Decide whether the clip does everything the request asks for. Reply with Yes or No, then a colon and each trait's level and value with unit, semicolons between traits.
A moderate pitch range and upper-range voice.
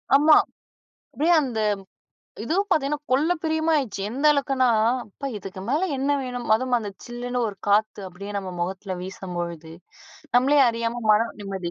No: wide, 6.1 semitones; high, 240 Hz